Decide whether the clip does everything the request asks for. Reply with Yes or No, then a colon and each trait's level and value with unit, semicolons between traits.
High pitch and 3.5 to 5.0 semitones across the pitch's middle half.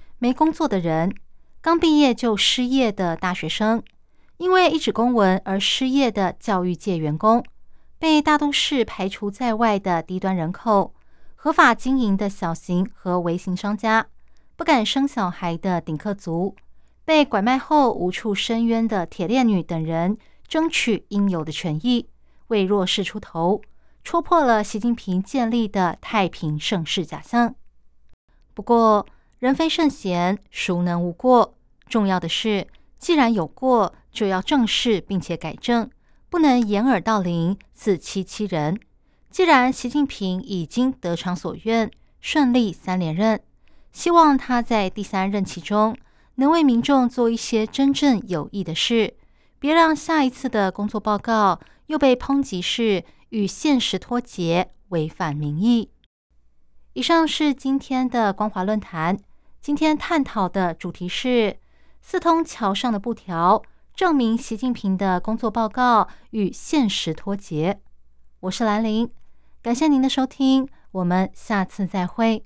No: high, 215 Hz; wide, 5.5 semitones